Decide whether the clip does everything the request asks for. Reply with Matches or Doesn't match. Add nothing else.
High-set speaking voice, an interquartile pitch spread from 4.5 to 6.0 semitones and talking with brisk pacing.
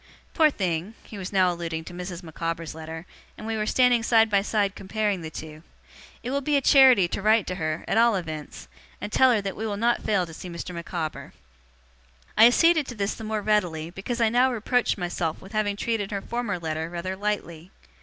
Matches